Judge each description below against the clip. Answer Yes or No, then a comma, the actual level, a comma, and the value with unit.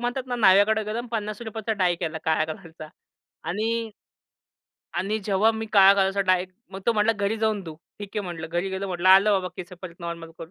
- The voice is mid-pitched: No, high, 200 Hz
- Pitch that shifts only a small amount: No, average, 3.5 semitones